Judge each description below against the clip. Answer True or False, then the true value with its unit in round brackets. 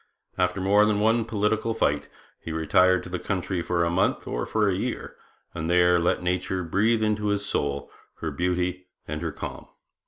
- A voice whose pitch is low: True (90 Hz)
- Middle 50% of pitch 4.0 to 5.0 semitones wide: False (3.2 semitones)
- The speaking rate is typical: True (185 wpm)